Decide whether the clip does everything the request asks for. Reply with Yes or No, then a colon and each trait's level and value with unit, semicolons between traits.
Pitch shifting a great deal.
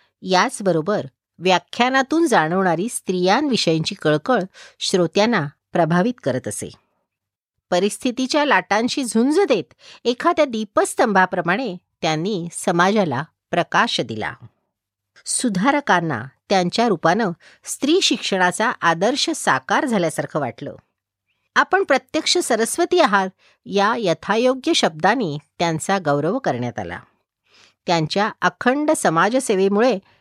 Yes: wide, 6.9 semitones